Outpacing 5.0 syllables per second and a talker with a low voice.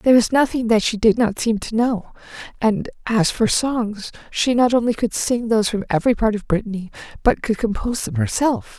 No: 5.4 syllables/s; high, 225 Hz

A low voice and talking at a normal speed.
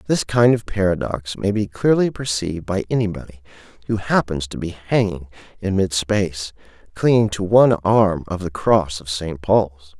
Yes: very low, 95 Hz; average, 170 wpm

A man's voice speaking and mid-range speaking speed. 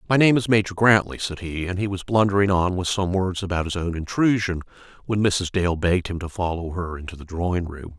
No: male; fast, 235 wpm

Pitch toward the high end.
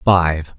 No: very low, 85 Hz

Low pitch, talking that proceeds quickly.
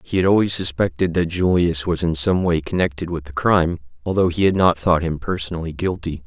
Yes: very low, 85 Hz; fast, 210 wpm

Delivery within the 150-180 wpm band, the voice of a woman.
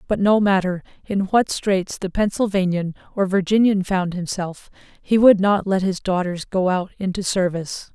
Yes: average, 165 wpm; female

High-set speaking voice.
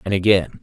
No: very low, 95 Hz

